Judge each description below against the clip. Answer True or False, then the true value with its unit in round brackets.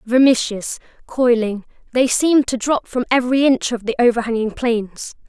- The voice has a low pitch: False (240 Hz)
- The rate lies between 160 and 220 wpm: False (150 wpm)